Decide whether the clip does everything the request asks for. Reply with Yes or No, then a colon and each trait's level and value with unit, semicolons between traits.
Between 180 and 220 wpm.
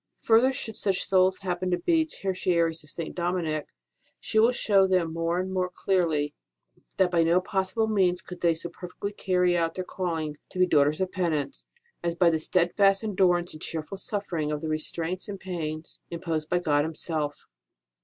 Yes: average, 185 wpm